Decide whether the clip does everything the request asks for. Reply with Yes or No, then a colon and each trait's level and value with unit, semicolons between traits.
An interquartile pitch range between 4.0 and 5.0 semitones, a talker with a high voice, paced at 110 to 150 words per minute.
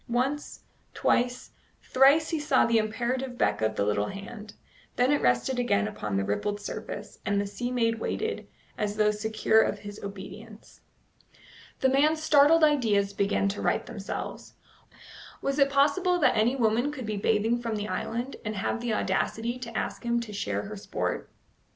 No: average, 4.3 semitones; high, 225 Hz; average, 170 wpm